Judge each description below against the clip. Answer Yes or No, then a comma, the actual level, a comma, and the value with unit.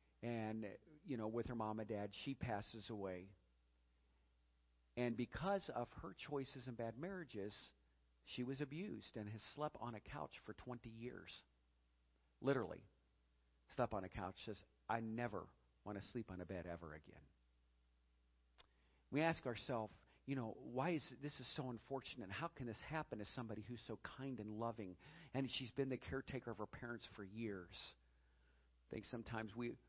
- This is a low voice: Yes, low, 110 Hz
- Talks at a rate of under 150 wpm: No, average, 170 wpm